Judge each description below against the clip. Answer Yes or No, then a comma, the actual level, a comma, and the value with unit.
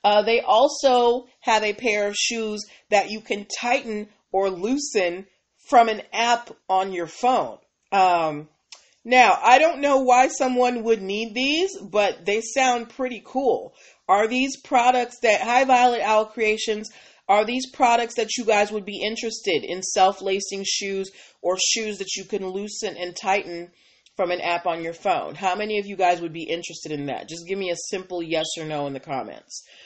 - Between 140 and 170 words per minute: No, average, 180 wpm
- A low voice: No, high, 210 Hz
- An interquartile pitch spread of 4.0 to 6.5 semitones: Yes, average, 4.3 semitones